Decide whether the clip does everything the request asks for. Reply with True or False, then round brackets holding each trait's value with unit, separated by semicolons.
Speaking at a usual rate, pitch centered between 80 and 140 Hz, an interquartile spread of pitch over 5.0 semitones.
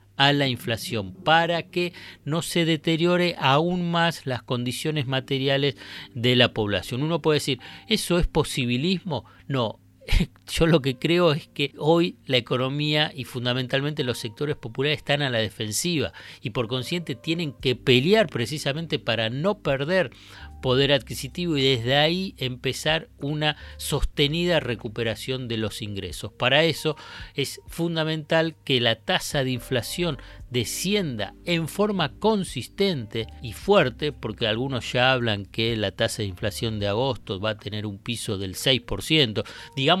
True (145 wpm; 135 Hz; 5.4 semitones)